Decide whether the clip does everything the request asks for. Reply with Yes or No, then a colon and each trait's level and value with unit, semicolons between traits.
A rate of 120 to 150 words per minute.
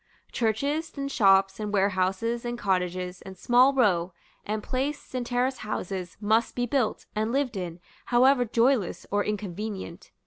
Yes: average, 145 wpm